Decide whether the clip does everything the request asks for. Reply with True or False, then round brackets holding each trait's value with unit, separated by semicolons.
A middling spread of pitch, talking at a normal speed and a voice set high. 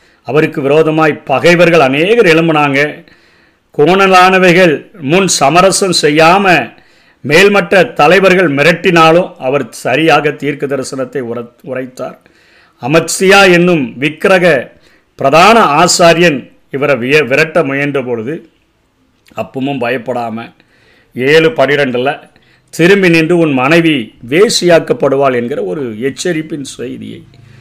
False (4.4 semitones; 85 wpm; 160 Hz)